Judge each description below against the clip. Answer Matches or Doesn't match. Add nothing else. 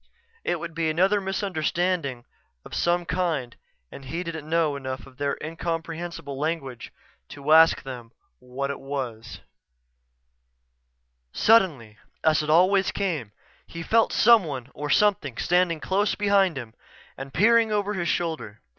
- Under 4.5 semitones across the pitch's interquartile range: Doesn't match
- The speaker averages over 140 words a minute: Doesn't match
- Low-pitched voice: Doesn't match